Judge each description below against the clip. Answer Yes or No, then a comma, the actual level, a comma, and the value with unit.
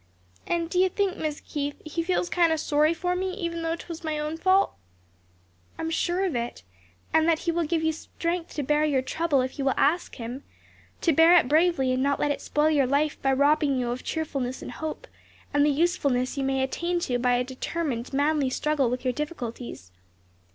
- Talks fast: Yes, fast, 215 wpm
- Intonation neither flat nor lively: Yes, average, 3.9 semitones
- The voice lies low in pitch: No, very high, 300 Hz